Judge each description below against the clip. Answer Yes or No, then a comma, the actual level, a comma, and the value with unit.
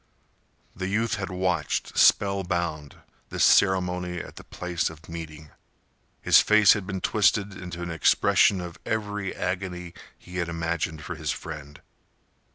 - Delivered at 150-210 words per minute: No, average, 140 wpm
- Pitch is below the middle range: Yes, very low, 90 Hz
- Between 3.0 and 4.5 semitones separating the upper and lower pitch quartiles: No, narrow, 2.5 semitones